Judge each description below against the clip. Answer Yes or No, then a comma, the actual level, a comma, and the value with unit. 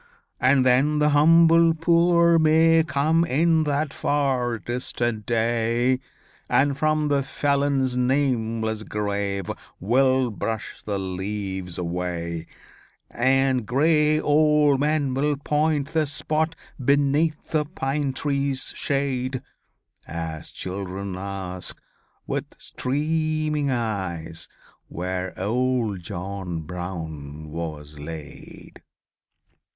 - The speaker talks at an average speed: No, slow, 95 wpm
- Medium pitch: No, low, 130 Hz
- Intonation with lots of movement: Yes, wide, 7.2 semitones